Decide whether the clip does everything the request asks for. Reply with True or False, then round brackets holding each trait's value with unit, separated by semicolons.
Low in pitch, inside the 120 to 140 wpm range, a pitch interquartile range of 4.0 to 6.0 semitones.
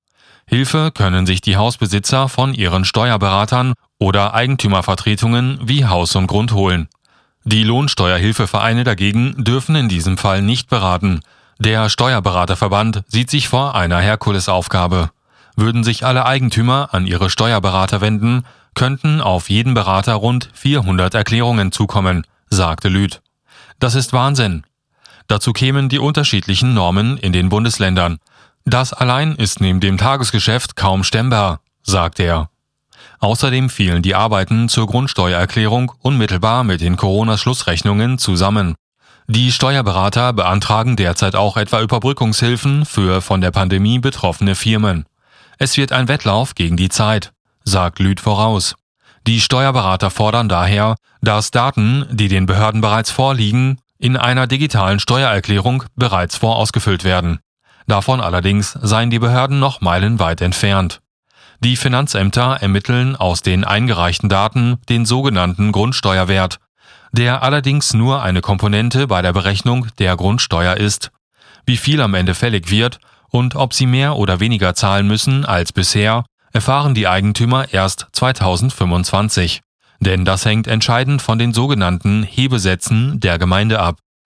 True (110 Hz; 130 wpm; 4.4 semitones)